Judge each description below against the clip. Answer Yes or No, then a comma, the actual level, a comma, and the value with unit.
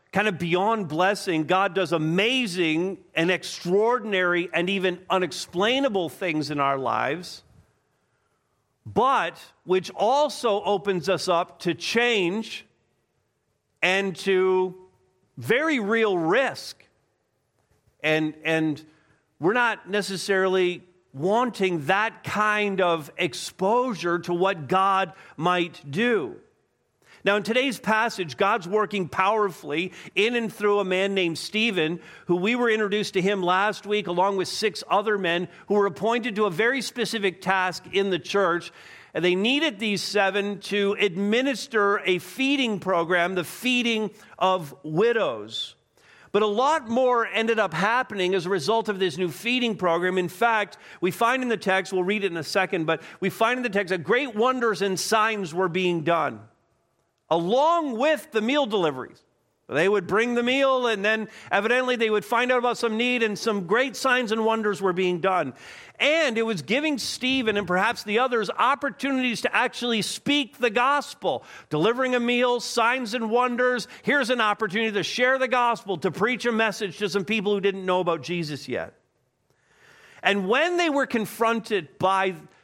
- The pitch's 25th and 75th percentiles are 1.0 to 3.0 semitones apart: No, average, 4.3 semitones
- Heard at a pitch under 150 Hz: No, high, 200 Hz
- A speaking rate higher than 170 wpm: No, average, 155 wpm